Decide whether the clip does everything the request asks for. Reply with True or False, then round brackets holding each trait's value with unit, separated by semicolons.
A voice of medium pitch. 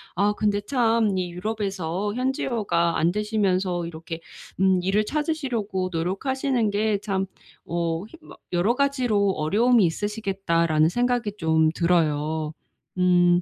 False (195 Hz)